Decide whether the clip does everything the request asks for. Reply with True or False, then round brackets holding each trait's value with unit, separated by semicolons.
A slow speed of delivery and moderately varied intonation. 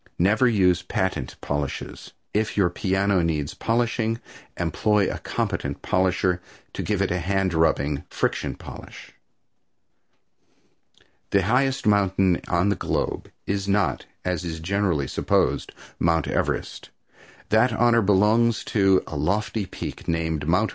True (125 wpm; 3.6 semitones)